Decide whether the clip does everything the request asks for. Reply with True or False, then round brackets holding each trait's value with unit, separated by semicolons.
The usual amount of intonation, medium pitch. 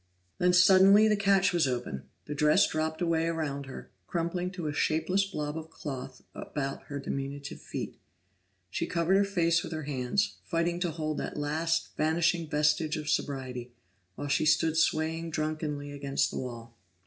True (3.1 semitones; 155 Hz)